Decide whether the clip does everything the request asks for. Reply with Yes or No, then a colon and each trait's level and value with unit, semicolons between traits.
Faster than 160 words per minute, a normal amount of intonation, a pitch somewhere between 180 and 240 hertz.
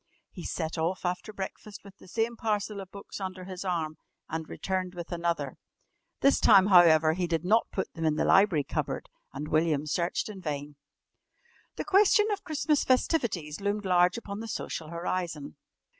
Yes: average, 175 wpm; average, 4.0 semitones; medium, 185 Hz